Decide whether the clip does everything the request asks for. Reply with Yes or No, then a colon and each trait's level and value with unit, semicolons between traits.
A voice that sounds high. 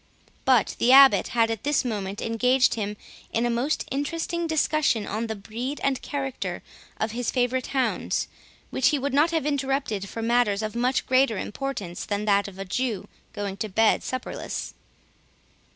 Yes: high, 240 Hz